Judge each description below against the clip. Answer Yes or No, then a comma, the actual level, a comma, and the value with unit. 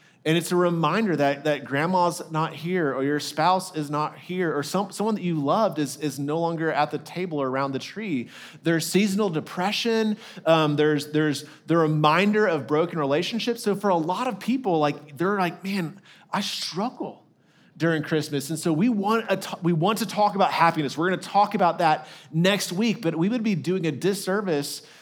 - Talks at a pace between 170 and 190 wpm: No, average, 200 wpm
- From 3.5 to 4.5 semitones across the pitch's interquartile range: Yes, average, 4.2 semitones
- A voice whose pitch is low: No, medium, 165 Hz